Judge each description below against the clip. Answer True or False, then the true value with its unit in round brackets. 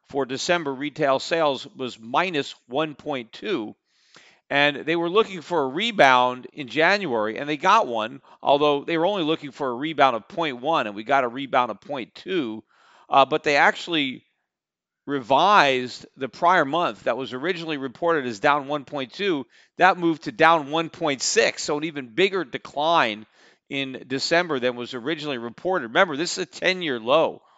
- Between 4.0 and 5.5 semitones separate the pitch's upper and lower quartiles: False (3.6 semitones)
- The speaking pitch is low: False (145 Hz)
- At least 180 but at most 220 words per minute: False (165 wpm)